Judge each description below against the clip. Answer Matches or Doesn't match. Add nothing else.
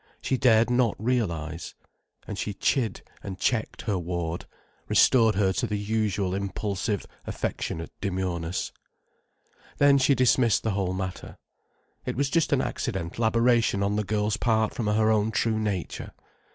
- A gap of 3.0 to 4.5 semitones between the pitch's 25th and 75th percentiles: Matches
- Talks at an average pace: Matches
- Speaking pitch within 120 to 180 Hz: Doesn't match